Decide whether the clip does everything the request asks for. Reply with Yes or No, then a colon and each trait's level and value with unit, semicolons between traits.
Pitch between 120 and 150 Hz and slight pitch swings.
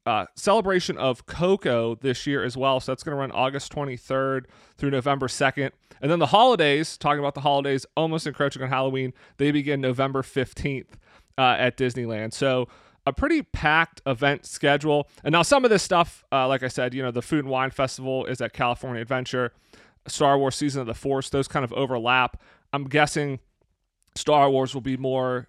Yes: low, 135 Hz; narrow, 2.2 semitones